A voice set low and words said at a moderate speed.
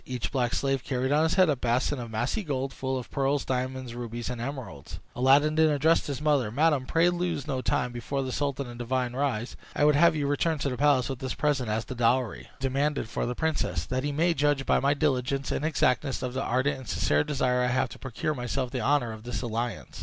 No: low, 130 Hz; fast, 235 wpm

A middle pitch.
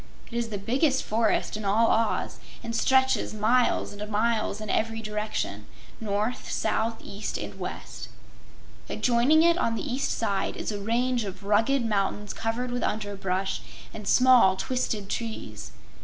No: high, 220 Hz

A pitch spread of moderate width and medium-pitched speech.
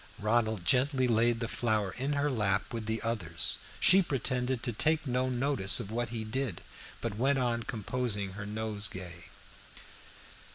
No: average, 3.2 semitones; low, 115 Hz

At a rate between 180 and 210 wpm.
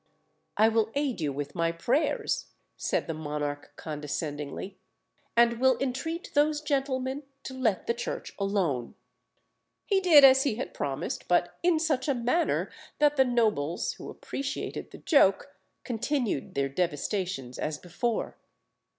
No: average, 140 wpm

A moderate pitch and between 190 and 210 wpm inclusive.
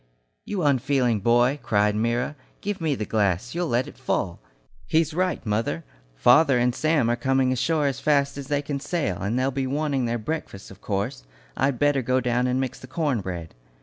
No: low, 130 Hz; average, 195 wpm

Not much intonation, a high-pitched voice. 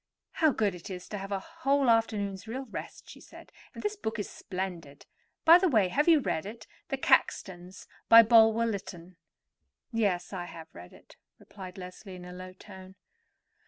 No: average, 4.1 semitones; high, 200 Hz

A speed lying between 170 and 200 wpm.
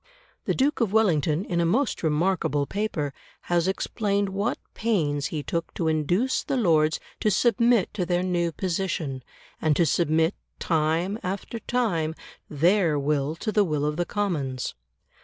No: average, 155 wpm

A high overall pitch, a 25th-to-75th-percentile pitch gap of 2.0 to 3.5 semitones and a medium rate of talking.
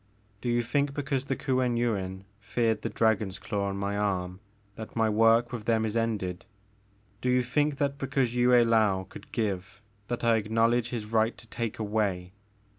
No: low, 115 Hz; average, 3.1 semitones; average, 180 wpm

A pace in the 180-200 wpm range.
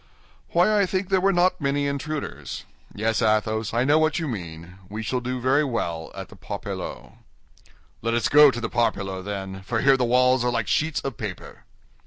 Yes: average, 195 wpm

